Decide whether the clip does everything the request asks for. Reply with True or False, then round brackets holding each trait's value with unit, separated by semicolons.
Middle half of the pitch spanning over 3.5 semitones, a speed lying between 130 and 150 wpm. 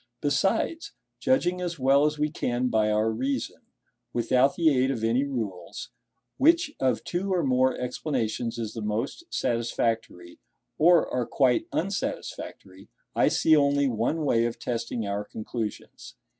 True (5.0 semitones; 145 wpm)